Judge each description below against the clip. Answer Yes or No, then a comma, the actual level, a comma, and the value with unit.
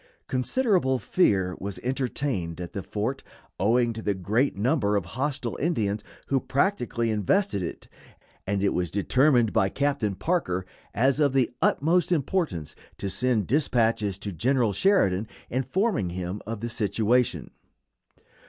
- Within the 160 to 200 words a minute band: No, slow, 135 wpm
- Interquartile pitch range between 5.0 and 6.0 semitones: Yes, wide, 5.5 semitones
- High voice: No, low, 115 Hz